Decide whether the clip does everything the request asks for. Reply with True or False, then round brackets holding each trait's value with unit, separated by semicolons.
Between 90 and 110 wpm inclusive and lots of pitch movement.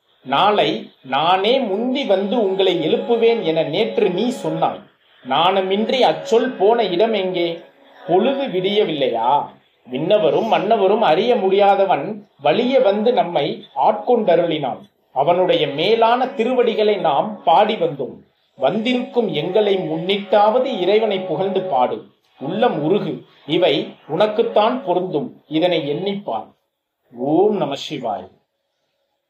False (95 wpm; 4.1 semitones)